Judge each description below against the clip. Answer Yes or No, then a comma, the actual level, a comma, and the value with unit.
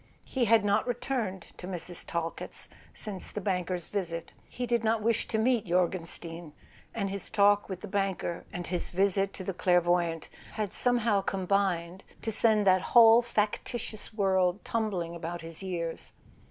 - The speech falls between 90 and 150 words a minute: No, average, 160 wpm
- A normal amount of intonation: Yes, average, 3.7 semitones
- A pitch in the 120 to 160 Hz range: No, high, 195 Hz